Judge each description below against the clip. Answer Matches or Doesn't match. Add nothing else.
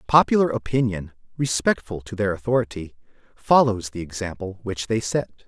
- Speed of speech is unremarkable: Doesn't match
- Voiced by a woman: Doesn't match